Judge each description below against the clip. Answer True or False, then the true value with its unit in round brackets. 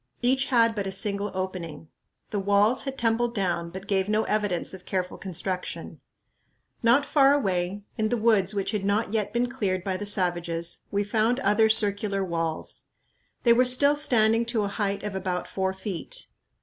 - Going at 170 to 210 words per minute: True (175 wpm)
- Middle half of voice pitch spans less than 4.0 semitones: True (3.4 semitones)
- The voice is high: True (205 Hz)